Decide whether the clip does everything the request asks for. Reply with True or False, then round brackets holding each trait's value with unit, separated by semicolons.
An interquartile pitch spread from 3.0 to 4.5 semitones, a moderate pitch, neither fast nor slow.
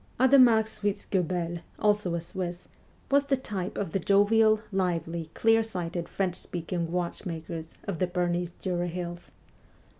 False (3.3 semitones; 180 Hz; 130 wpm)